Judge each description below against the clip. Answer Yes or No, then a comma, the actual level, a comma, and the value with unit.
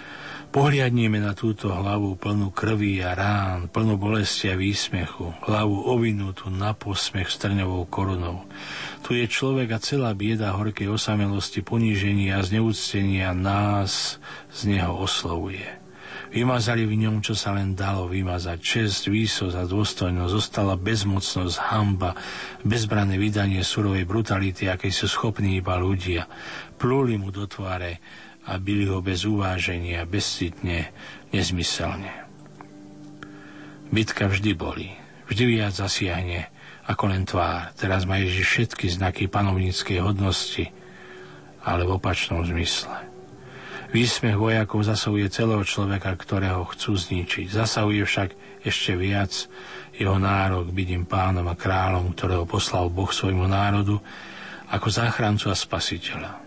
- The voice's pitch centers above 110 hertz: No, low, 100 Hz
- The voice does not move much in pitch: Yes, narrow, 2.3 semitones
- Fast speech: No, average, 120 wpm